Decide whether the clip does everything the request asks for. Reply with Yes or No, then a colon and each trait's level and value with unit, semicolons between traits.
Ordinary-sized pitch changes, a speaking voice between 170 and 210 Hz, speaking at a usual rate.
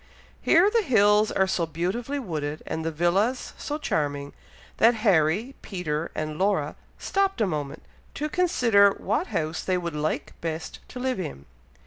No: wide, 7.5 semitones; high, 190 Hz; average, 155 wpm